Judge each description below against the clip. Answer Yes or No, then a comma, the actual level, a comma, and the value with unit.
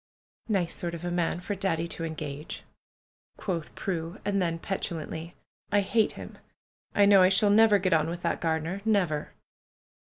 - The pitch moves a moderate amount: Yes, average, 3.3 semitones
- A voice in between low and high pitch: Yes, medium, 175 Hz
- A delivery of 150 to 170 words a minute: Yes, average, 165 wpm